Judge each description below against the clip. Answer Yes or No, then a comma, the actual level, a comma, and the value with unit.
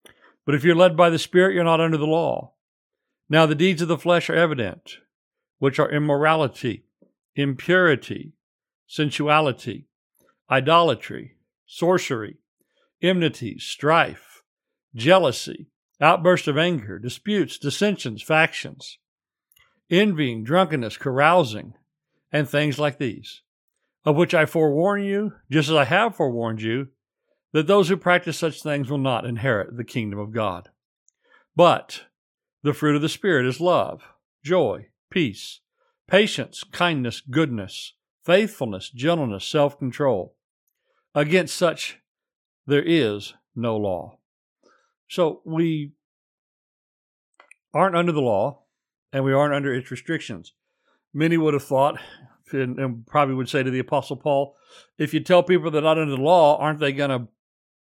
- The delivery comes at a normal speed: No, slow, 130 wpm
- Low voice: No, medium, 150 Hz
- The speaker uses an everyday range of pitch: Yes, average, 4.3 semitones